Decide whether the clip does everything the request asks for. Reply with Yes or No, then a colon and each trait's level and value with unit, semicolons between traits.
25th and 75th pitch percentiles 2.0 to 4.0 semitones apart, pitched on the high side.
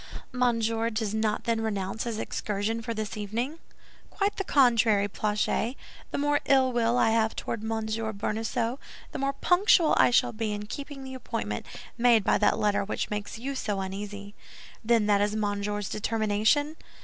Yes: average, 2.9 semitones; high, 220 Hz